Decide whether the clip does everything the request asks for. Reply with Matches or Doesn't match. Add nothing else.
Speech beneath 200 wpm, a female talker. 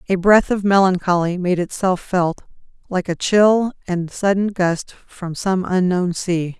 Matches